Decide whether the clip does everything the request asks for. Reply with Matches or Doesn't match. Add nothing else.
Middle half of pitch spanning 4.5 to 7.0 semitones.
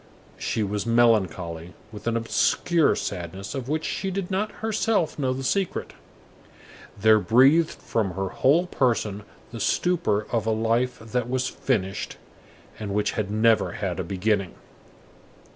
Matches